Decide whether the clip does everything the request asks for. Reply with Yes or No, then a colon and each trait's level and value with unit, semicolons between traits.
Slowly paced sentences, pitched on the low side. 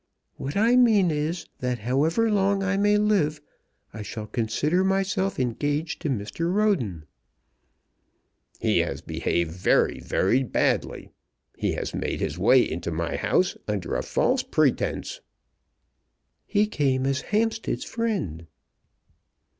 No: slow, 125 wpm; medium, 150 Hz